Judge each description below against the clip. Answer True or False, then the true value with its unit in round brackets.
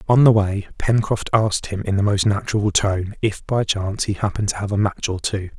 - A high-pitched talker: False (100 Hz)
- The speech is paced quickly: True (235 wpm)